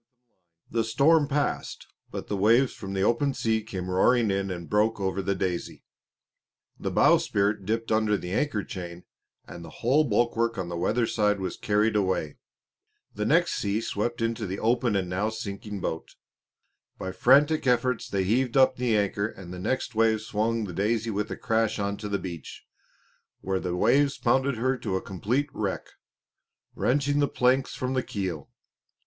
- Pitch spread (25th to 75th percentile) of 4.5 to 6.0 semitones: No, average, 4.0 semitones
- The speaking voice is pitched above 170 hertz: No, low, 110 Hz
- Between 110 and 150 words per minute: No, average, 170 wpm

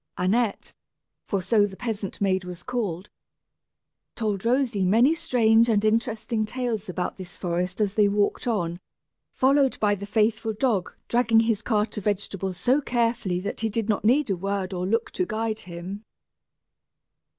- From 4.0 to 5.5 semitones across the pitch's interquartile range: No, average, 3.2 semitones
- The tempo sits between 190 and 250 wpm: No, average, 160 wpm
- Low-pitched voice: No, high, 215 Hz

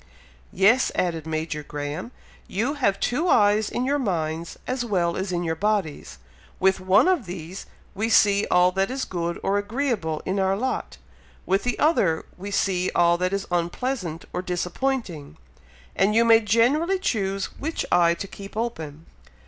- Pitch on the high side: Yes, high, 195 Hz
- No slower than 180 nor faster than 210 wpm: No, average, 165 wpm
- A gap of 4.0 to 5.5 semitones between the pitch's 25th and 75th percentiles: Yes, average, 5.1 semitones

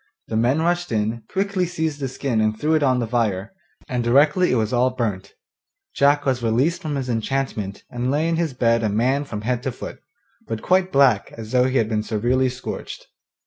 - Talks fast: Yes, fast, 210 wpm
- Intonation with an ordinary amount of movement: Yes, average, 4.3 semitones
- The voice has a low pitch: Yes, low, 125 Hz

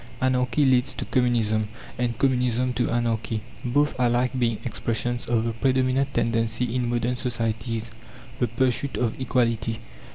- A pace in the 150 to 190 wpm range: No, slow, 135 wpm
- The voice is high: No, low, 120 Hz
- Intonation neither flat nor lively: No, narrow, 1.8 semitones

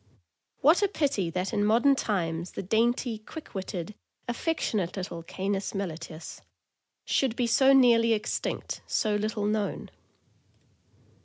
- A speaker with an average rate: No, slow, 125 wpm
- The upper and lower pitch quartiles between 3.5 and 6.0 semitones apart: Yes, average, 4.2 semitones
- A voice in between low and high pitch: No, high, 215 Hz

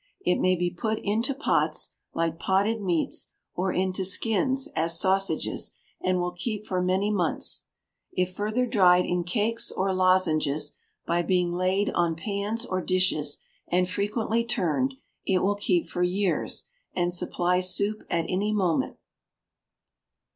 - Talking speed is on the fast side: No, average, 140 wpm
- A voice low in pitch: No, medium, 185 Hz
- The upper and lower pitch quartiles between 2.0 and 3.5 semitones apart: Yes, average, 2.8 semitones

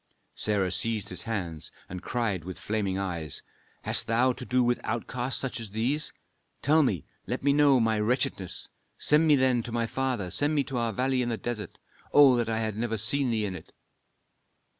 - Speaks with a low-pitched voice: Yes, low, 115 Hz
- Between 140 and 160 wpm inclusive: No, average, 195 wpm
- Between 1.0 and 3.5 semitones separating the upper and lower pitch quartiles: No, average, 4.0 semitones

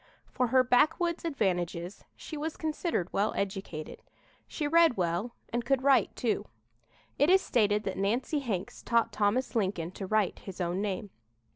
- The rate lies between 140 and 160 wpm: Yes, average, 155 wpm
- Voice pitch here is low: No, high, 220 Hz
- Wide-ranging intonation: Yes, wide, 6.4 semitones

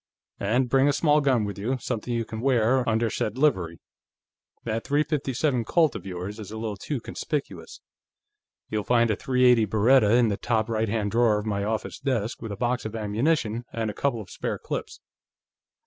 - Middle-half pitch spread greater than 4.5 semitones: No, average, 3.4 semitones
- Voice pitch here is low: Yes, low, 115 Hz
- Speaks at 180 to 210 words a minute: Yes, average, 190 wpm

